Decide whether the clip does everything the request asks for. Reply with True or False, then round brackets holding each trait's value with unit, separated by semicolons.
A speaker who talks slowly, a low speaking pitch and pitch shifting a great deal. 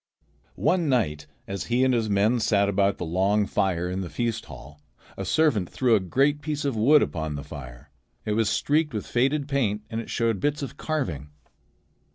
False (195 wpm; 110 Hz; 6.4 semitones)